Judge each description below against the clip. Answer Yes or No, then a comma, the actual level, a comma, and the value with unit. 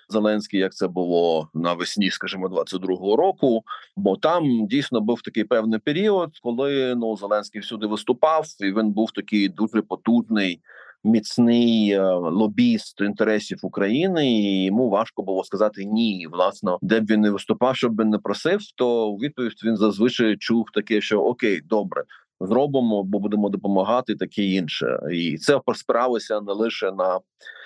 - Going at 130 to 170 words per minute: Yes, average, 150 wpm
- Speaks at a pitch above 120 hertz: No, low, 110 Hz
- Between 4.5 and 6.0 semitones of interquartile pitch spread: No, average, 2.9 semitones